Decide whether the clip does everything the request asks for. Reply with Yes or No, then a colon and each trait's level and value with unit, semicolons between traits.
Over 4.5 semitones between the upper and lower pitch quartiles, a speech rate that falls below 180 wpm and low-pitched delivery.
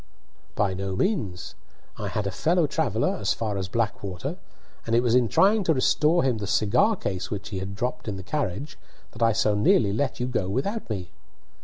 No: wide, 5.6 semitones; fast, 205 wpm; low, 110 Hz